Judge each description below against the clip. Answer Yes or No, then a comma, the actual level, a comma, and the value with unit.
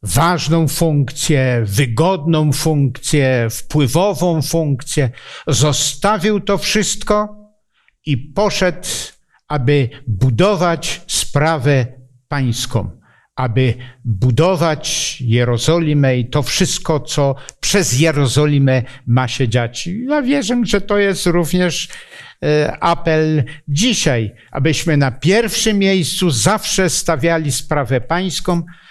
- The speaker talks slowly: Yes, slow, 90 wpm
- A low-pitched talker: No, medium, 155 Hz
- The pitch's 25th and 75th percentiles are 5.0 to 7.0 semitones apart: Yes, wide, 5.4 semitones